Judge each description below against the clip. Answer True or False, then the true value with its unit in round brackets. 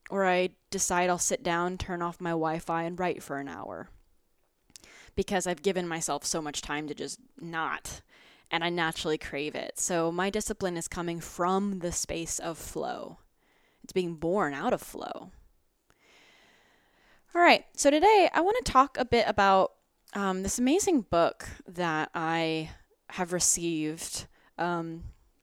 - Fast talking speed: False (155 wpm)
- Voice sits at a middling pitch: True (175 Hz)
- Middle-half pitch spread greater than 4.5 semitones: False (3.1 semitones)